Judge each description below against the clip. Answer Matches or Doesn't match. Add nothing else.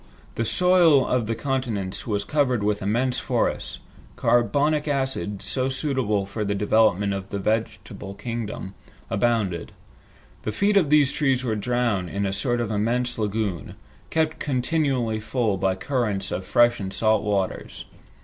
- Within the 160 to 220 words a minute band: Doesn't match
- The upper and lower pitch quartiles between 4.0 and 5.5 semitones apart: Matches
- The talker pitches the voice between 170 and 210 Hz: Doesn't match